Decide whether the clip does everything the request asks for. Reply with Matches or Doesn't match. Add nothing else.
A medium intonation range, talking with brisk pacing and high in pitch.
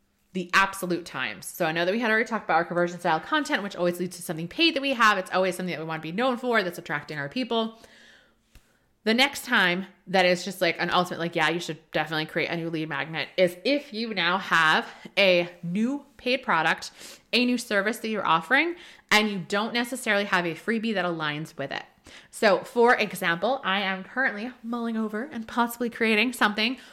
Matches